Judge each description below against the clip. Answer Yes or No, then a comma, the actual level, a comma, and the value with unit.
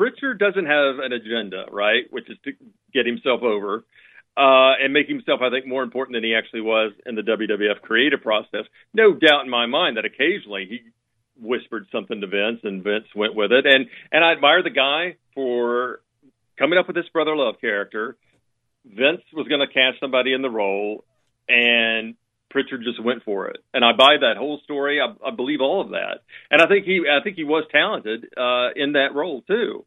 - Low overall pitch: Yes, low, 130 Hz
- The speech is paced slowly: No, fast, 205 wpm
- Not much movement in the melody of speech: No, average, 4.1 semitones